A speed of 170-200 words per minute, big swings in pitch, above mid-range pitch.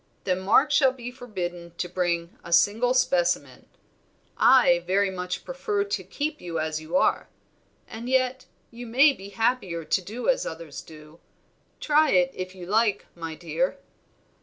No: average, 160 wpm; wide, 6.7 semitones; high, 195 Hz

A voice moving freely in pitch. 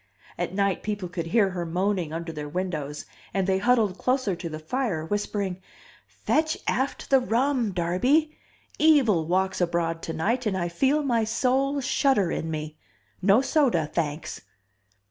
Yes: wide, 6.8 semitones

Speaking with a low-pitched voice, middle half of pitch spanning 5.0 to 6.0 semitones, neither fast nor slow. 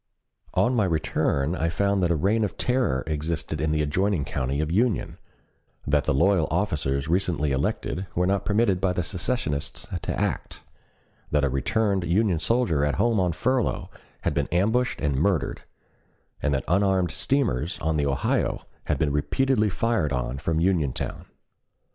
Yes: very low, 85 Hz; wide, 5.5 semitones; average, 160 wpm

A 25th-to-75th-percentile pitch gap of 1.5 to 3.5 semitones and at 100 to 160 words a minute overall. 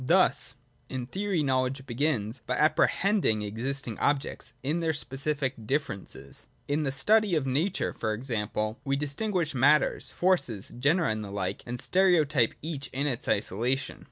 No: average, 4.6 semitones; average, 145 wpm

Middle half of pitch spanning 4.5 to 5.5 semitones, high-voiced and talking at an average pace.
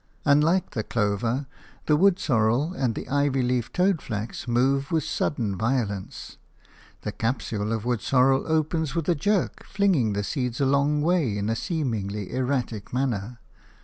No: average, 4.9 semitones; low, 130 Hz; average, 150 wpm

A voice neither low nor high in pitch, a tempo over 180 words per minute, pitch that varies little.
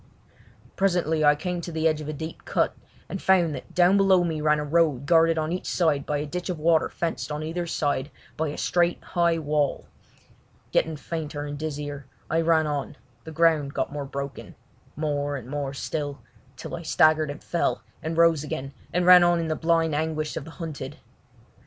Yes: medium, 155 Hz; average, 195 wpm; narrow, 2.3 semitones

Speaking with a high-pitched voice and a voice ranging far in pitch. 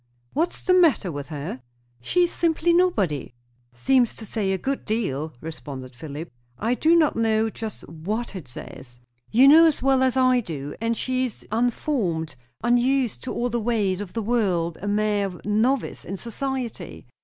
Yes: high, 220 Hz; wide, 7.1 semitones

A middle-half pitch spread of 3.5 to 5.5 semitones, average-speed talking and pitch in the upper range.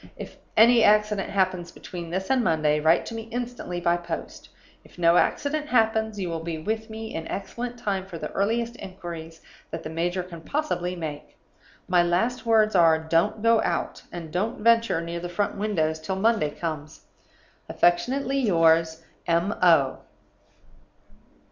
No: average, 5.0 semitones; average, 160 wpm; medium, 180 Hz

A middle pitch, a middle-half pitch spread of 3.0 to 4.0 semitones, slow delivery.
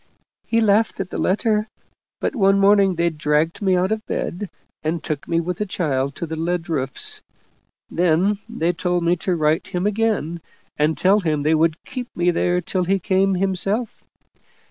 No: medium, 180 Hz; average, 3.3 semitones; average, 185 wpm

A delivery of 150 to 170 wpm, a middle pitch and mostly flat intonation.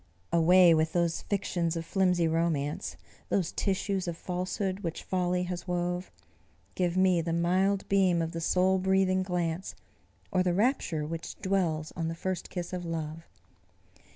Yes: average, 155 wpm; medium, 180 Hz; narrow, 2.1 semitones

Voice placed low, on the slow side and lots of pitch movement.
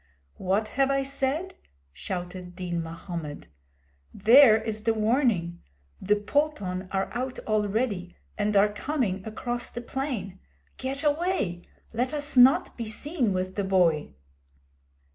No: high, 215 Hz; slow, 125 wpm; wide, 6.2 semitones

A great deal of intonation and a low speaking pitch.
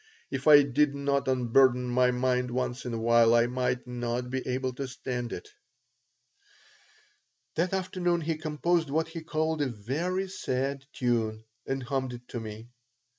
No: average, 3.5 semitones; low, 130 Hz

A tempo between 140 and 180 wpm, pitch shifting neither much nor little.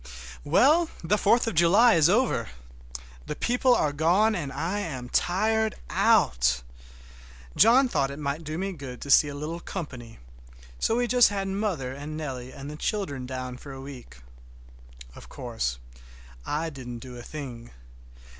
No: average, 160 wpm; wide, 7.6 semitones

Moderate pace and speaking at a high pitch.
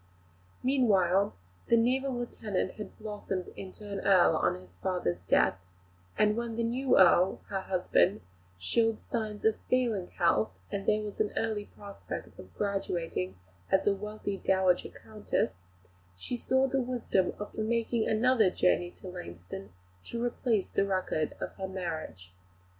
Yes: average, 145 wpm; high, 200 Hz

